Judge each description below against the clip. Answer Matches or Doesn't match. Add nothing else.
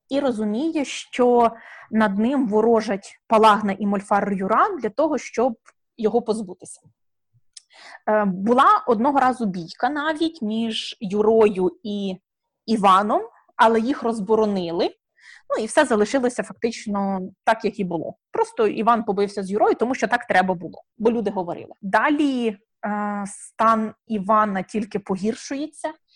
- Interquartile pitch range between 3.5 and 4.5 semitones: Doesn't match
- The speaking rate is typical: Matches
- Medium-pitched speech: Doesn't match